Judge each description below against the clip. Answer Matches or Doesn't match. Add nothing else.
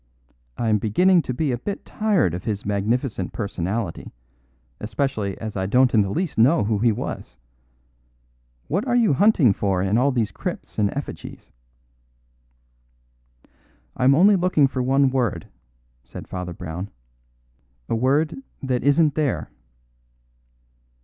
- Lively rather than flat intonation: Matches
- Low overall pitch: Matches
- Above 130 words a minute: Matches